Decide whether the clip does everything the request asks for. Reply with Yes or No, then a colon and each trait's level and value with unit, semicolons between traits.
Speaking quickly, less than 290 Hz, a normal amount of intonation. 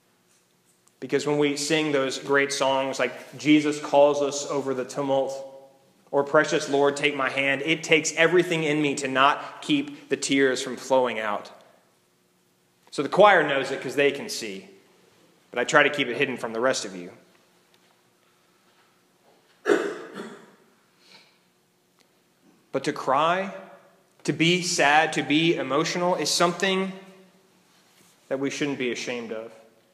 No: average, 140 wpm; medium, 140 Hz; average, 3.8 semitones